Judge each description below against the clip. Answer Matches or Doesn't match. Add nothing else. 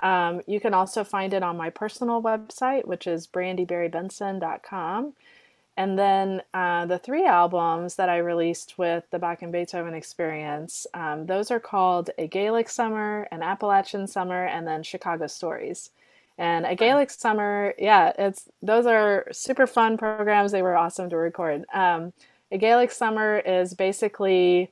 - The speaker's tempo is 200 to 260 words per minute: Doesn't match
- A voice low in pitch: Doesn't match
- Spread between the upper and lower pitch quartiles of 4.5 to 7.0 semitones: Doesn't match